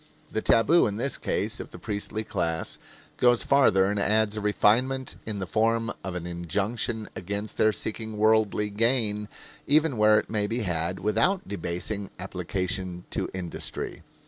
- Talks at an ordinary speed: Yes, average, 155 wpm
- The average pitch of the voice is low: Yes, low, 105 Hz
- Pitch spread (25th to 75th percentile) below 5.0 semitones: Yes, average, 3.0 semitones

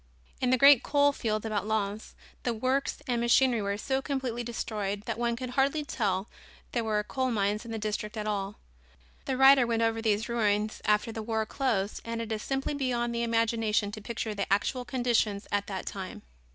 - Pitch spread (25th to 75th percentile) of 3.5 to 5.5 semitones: No, average, 2.9 semitones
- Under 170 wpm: No, average, 195 wpm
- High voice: Yes, high, 225 Hz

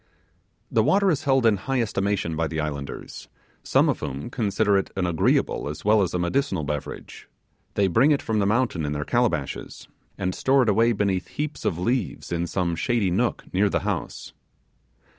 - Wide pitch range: Yes, wide, 5.7 semitones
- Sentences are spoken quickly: No, average, 185 wpm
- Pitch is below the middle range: Yes, low, 100 Hz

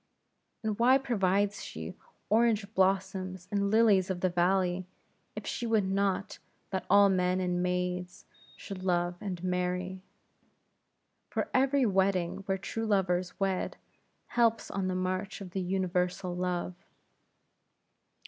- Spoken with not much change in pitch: Yes, narrow, 1.9 semitones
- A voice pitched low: No, high, 190 Hz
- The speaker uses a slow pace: Yes, slow, 125 wpm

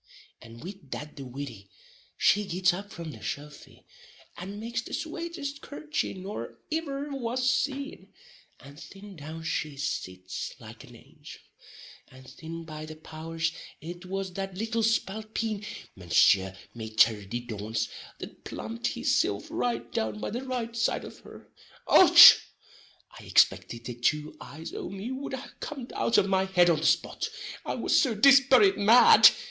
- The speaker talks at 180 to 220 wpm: No, average, 160 wpm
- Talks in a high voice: No, medium, 180 Hz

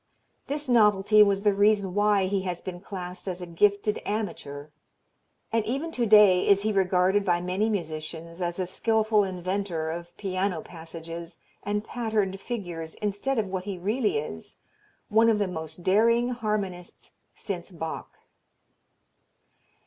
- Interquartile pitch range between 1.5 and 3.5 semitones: Yes, average, 3.2 semitones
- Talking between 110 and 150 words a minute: Yes, average, 145 wpm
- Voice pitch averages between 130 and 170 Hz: No, high, 195 Hz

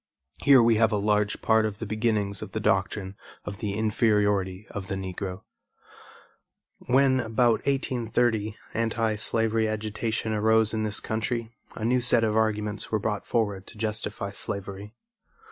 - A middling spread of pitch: No, narrow, 1.7 semitones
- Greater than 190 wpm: No, average, 150 wpm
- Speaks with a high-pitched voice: No, low, 110 Hz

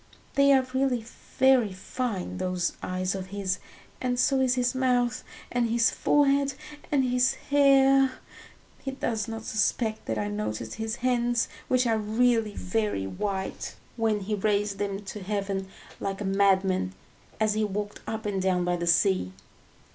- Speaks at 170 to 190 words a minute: No, average, 155 wpm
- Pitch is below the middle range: No, high, 215 Hz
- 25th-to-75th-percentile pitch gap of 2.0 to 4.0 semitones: No, average, 4.5 semitones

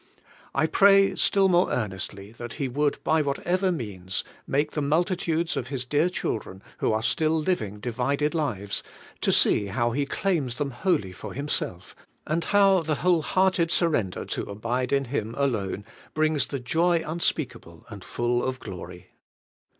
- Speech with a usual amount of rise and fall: No, wide, 6.5 semitones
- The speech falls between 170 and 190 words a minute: No, average, 160 wpm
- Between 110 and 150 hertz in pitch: Yes, medium, 140 Hz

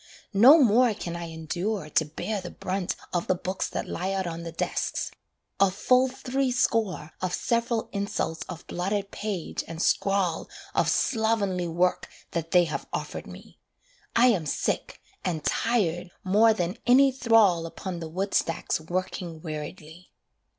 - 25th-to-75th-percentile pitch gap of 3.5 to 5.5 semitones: Yes, average, 4.6 semitones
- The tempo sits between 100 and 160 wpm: Yes, average, 150 wpm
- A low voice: No, medium, 185 Hz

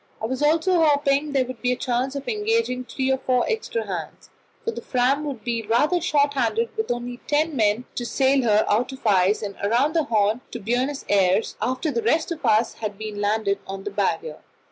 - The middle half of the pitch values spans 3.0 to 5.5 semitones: Yes, average, 4.8 semitones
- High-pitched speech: Yes, very high, 250 Hz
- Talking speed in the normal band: No, fast, 220 wpm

